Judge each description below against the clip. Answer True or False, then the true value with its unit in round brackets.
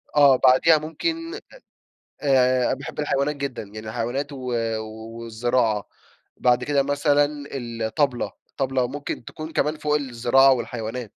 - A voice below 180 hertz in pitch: True (135 Hz)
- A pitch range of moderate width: True (3.2 semitones)